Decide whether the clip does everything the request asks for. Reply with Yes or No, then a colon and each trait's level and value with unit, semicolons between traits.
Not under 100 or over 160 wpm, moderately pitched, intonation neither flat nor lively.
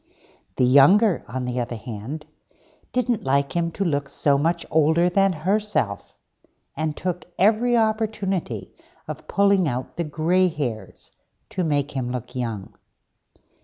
No: slow, 135 wpm; medium, 155 Hz; wide, 6.6 semitones